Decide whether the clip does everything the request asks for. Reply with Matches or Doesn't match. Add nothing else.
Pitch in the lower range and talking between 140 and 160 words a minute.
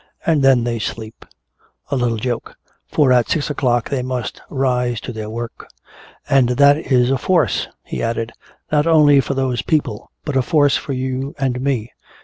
Doesn't match